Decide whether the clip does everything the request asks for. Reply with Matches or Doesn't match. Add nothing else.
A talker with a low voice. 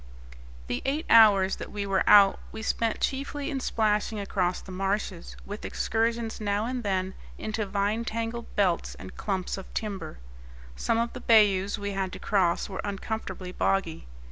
Doesn't match